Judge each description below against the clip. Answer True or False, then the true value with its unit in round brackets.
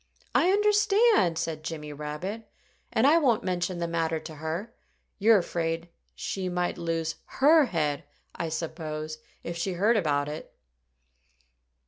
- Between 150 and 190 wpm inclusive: False (135 wpm)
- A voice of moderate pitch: True (170 Hz)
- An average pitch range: False (5.8 semitones)